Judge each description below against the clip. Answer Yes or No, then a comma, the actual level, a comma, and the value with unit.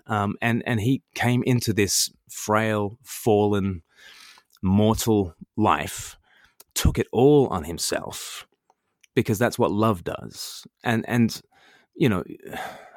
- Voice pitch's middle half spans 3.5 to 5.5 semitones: No, average, 2.7 semitones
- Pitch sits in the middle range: No, low, 110 Hz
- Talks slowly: Yes, slow, 115 wpm